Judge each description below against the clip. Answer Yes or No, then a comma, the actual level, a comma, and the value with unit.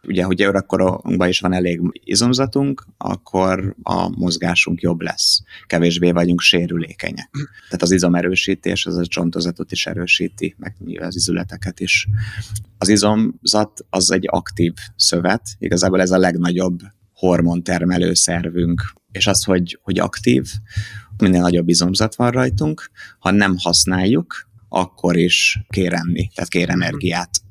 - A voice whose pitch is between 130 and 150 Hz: No, very low, 90 Hz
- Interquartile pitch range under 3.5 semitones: Yes, average, 2.7 semitones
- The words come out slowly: No, average, 130 wpm